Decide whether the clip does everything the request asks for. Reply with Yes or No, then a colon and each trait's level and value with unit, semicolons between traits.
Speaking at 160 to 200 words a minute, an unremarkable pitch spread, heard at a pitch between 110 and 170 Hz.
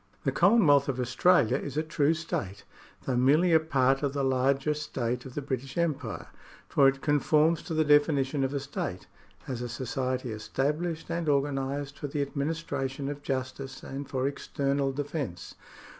No: average, 165 wpm; narrow, 2.2 semitones; medium, 140 Hz